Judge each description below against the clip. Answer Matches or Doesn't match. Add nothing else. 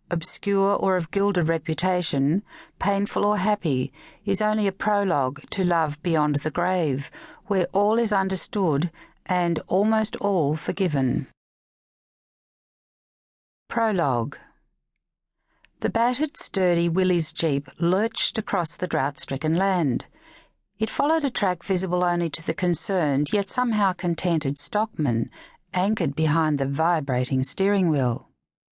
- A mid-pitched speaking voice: Matches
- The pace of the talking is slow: Matches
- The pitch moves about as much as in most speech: Matches